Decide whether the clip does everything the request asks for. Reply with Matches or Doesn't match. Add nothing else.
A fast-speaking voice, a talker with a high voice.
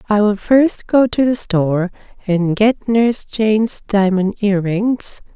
Doesn't match